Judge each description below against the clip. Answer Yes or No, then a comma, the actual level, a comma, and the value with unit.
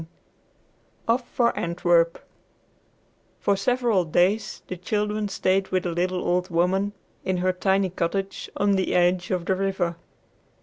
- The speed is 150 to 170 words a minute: No, average, 140 wpm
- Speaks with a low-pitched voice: No, medium, 185 Hz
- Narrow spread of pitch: Yes, narrow, 2.1 semitones